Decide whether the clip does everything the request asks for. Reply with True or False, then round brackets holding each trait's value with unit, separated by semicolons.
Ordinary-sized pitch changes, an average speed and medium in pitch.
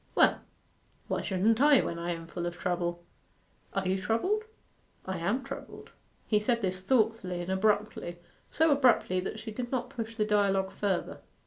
False (4.0 semitones; 170 wpm; 205 Hz)